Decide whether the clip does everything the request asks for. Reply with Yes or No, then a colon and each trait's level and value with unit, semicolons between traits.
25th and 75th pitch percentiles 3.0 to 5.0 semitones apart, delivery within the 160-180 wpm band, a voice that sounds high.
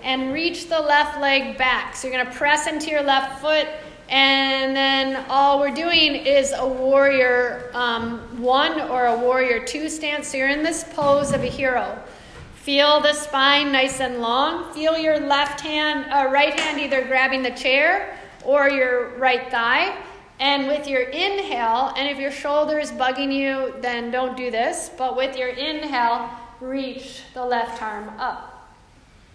No: narrow, 2.6 semitones; average, 170 wpm; very high, 270 Hz